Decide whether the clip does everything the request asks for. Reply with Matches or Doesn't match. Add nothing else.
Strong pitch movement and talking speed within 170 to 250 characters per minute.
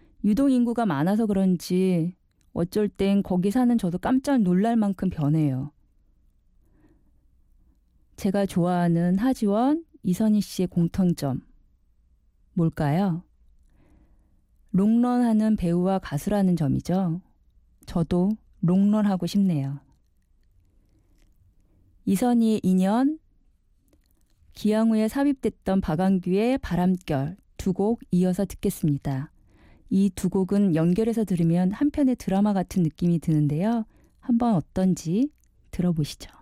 Doesn't match